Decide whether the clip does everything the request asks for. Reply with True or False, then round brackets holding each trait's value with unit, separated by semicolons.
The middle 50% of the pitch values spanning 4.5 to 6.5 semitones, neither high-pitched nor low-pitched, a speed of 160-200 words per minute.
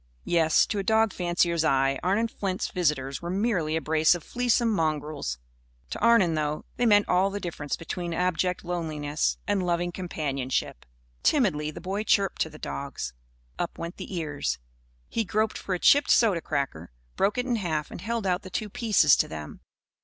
True (4.9 semitones; 175 Hz; 180 wpm)